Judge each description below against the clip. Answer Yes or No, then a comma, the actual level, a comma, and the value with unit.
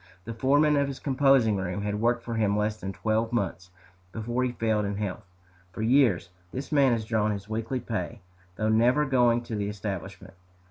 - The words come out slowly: No, average, 190 wpm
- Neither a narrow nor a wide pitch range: Yes, average, 3.1 semitones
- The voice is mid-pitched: No, low, 110 Hz